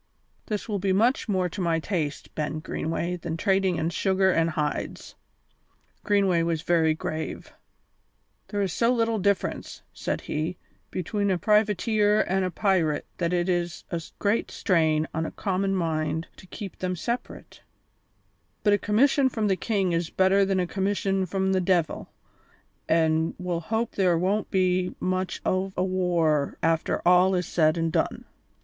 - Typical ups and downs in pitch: Yes, average, 3.1 semitones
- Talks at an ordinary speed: Yes, average, 160 wpm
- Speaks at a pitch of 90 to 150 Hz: No, medium, 185 Hz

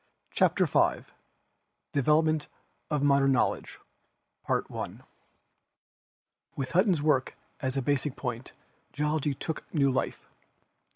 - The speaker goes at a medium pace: No, slow, 100 wpm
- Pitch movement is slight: Yes, narrow, 2.3 semitones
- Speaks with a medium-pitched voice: Yes, medium, 145 Hz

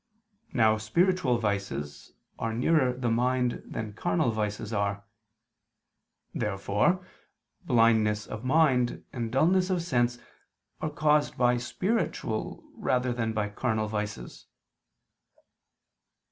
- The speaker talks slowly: Yes, slow, 105 wpm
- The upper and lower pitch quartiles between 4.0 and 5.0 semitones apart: No, average, 3.6 semitones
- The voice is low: Yes, low, 120 Hz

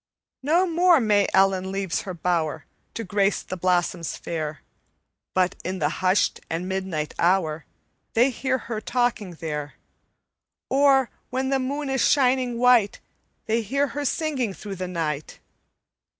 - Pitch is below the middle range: No, high, 200 Hz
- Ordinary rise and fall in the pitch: No, wide, 6.5 semitones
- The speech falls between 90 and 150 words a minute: Yes, average, 140 wpm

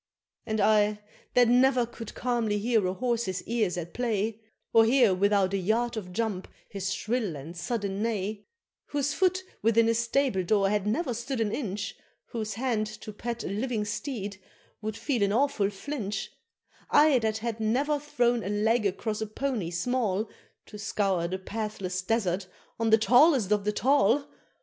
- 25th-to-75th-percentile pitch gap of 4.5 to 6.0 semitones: No, average, 3.3 semitones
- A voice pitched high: Yes, high, 220 Hz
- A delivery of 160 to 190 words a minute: Yes, average, 170 wpm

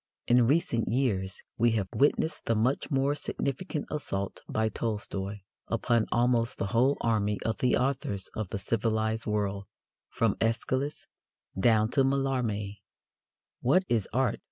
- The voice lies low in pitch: Yes, low, 115 Hz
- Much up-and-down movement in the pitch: No, average, 4.0 semitones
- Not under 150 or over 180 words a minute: No, slow, 135 wpm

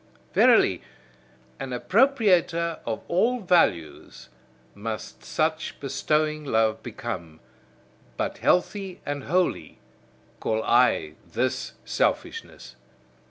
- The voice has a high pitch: No, medium, 150 Hz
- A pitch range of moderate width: No, wide, 8.2 semitones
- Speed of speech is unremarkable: No, slow, 85 wpm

